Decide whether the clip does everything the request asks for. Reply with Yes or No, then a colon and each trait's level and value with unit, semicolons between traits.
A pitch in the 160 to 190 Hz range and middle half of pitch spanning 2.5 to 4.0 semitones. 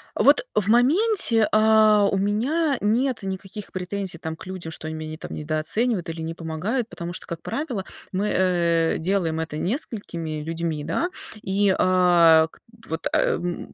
No: medium, 185 Hz; average, 4.8 semitones